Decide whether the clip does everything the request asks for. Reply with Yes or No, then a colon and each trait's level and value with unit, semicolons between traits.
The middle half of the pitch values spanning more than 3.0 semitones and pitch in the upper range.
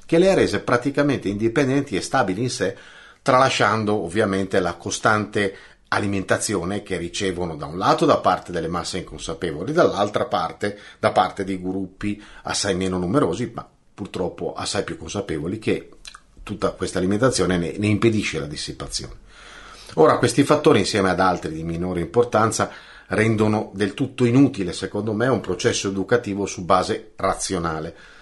No: average, 4.2 semitones; low, 100 Hz